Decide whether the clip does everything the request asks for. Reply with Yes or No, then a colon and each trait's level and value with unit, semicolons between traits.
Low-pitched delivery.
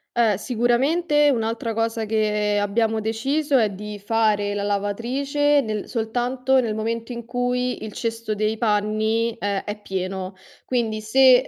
No: high, 225 Hz